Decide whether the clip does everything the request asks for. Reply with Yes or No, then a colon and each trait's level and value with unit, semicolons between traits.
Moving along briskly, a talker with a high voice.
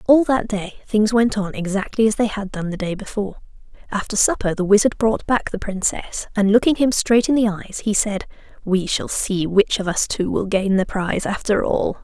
Yes: fast, 220 wpm; high, 210 Hz